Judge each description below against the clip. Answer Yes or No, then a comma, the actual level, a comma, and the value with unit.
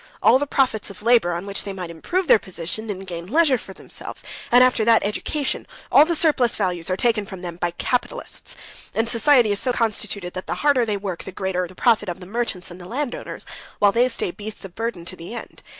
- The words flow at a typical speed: No, fast, 225 wpm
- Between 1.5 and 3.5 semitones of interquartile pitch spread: No, average, 4.9 semitones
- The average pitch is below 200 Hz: No, high, 210 Hz